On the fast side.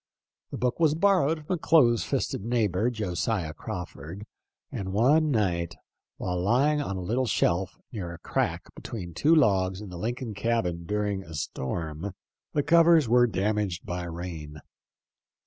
No: average, 150 wpm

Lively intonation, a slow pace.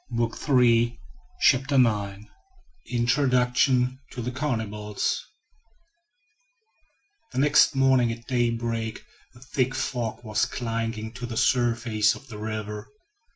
No: narrow, 2.4 semitones; slow, 100 wpm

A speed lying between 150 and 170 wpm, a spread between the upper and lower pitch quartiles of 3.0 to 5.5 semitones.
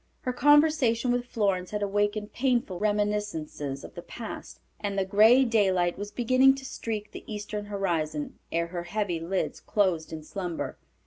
Yes: average, 155 wpm; average, 4.3 semitones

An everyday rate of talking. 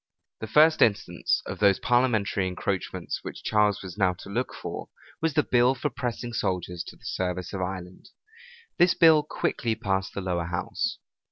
Yes: average, 170 wpm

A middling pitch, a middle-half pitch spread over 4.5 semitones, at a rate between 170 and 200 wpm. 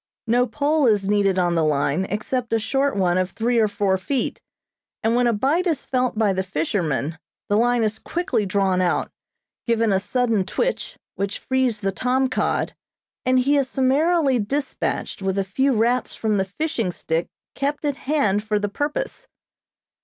No: high, 225 Hz; average, 5.2 semitones; average, 175 wpm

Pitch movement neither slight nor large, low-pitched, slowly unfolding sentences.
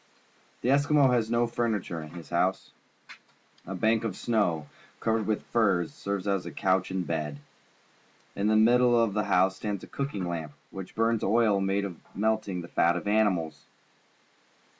No: average, 4.0 semitones; low, 100 Hz; average, 160 wpm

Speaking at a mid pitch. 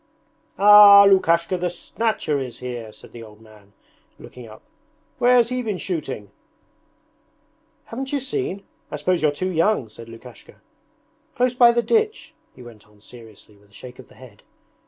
Yes: medium, 160 Hz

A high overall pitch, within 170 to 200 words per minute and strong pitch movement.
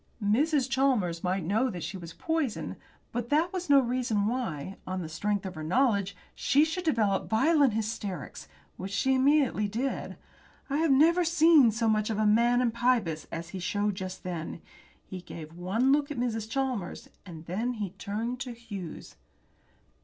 Yes: high, 225 Hz; average, 175 wpm; wide, 5.8 semitones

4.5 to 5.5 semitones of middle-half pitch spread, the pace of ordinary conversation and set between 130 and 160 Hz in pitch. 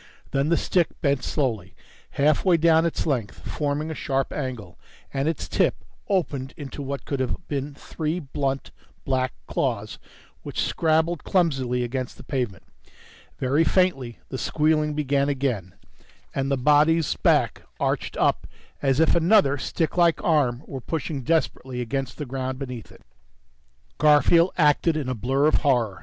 No: average, 3.3 semitones; average, 150 wpm; medium, 140 Hz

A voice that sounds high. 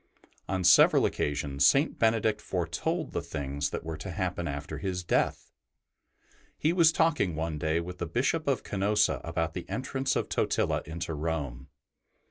No: very low, 85 Hz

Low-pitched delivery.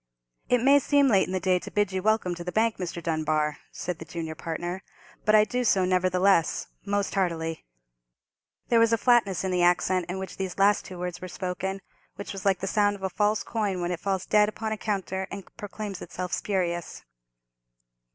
No: high, 190 Hz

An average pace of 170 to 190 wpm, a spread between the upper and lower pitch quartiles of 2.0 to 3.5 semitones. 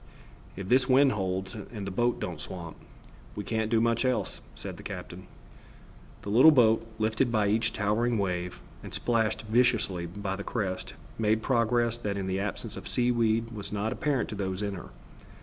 Yes: average, 180 wpm; average, 3.2 semitones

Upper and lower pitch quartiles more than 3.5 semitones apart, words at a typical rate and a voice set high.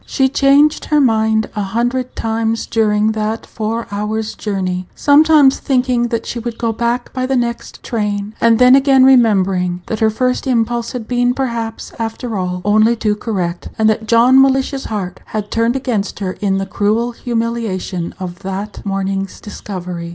No: average, 3.1 semitones; average, 165 wpm; high, 225 Hz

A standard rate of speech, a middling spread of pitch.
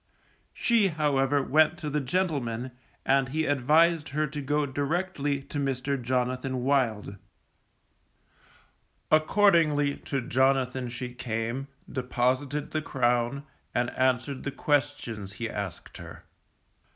No: slow, 115 wpm; average, 3.0 semitones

